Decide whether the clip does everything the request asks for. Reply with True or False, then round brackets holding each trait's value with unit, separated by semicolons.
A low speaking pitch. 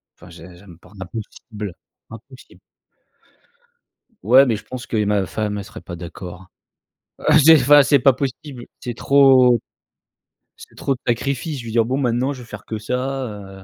True (120 Hz)